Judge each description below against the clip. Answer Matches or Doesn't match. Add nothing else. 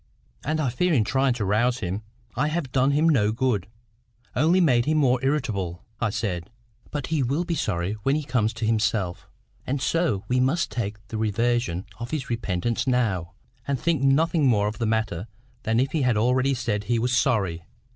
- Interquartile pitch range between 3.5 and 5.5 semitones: Matches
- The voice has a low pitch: Matches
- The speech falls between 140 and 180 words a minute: Doesn't match